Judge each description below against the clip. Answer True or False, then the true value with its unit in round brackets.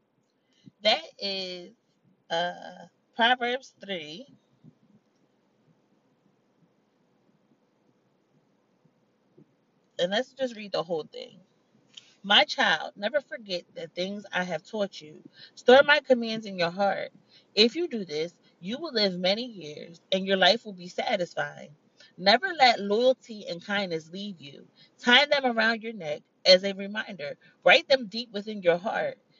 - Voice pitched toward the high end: True (210 Hz)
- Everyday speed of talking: False (130 wpm)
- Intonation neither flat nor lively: False (5.7 semitones)